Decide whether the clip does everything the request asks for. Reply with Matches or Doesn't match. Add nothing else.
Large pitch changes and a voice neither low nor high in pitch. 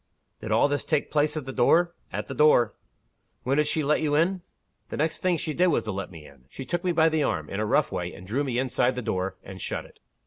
Matches